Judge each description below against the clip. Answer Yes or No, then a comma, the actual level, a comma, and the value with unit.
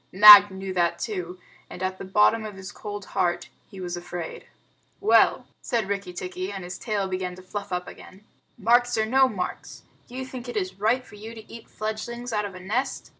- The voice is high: Yes, high, 200 Hz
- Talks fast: Yes, fast, 210 wpm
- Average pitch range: Yes, average, 3.1 semitones